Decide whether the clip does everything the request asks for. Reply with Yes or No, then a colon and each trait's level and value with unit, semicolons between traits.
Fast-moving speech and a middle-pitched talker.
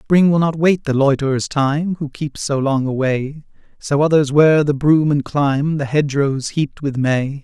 No: average, 195 wpm; medium, 145 Hz